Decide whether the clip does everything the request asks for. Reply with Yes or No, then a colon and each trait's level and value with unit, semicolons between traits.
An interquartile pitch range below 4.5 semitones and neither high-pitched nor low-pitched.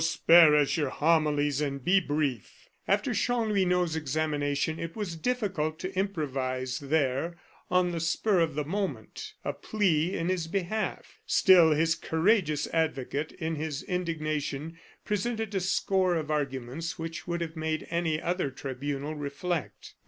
Yes: average, 3.5 semitones; medium, 160 Hz